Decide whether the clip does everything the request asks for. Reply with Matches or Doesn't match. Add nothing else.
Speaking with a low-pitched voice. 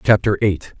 Matches